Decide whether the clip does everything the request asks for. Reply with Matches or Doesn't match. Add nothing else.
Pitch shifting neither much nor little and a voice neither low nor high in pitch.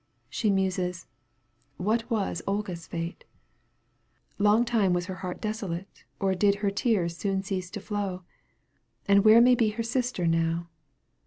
Doesn't match